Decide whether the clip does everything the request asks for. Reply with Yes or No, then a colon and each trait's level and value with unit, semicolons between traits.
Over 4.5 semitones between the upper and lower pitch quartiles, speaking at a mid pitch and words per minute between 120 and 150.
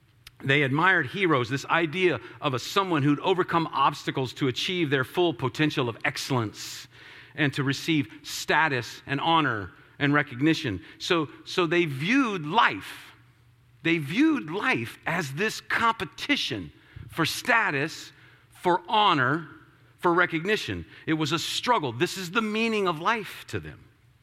Yes: average, 5.0 semitones; medium, 155 Hz; slow, 135 wpm